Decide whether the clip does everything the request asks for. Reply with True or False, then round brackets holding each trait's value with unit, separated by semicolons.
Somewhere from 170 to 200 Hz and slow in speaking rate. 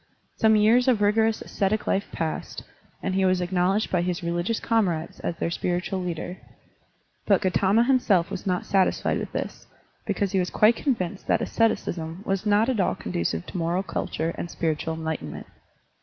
False (185 Hz; 170 wpm)